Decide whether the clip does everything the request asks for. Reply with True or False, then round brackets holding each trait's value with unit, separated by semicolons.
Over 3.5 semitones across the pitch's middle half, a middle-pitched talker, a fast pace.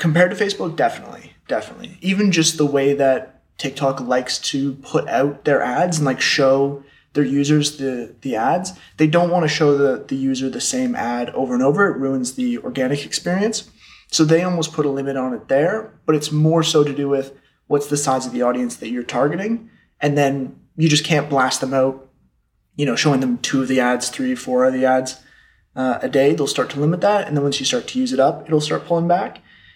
True (4.1 semitones; 145 Hz; 225 wpm)